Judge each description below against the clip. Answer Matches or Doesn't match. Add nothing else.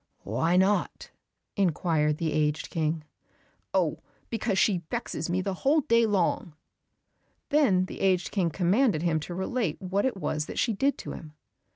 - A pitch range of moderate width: Matches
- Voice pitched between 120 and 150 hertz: Doesn't match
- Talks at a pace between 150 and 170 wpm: Matches